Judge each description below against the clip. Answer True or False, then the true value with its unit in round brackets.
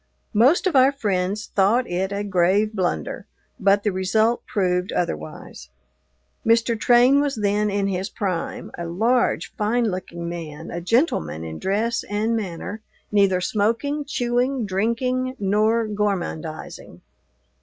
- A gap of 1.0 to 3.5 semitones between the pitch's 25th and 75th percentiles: False (4.2 semitones)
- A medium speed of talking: False (130 wpm)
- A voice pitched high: True (205 Hz)